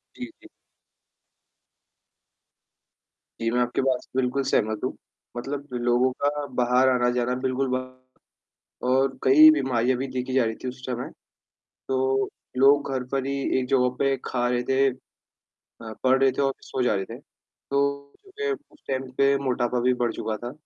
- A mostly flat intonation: Yes, narrow, 1.7 semitones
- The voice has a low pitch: Yes, low, 130 Hz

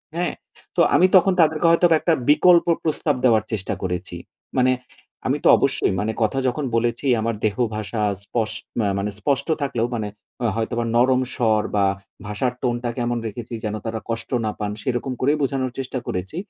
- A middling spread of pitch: Yes, average, 4.2 semitones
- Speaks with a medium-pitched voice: No, low, 120 Hz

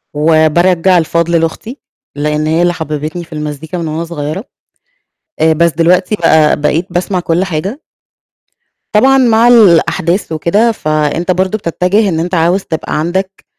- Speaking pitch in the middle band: Yes, medium, 170 Hz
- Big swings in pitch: No, average, 3.0 semitones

